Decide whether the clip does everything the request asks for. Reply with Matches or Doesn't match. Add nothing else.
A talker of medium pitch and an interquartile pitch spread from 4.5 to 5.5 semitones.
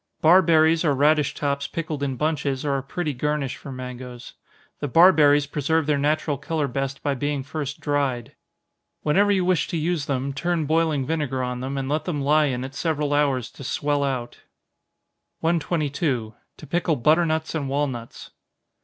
Doesn't match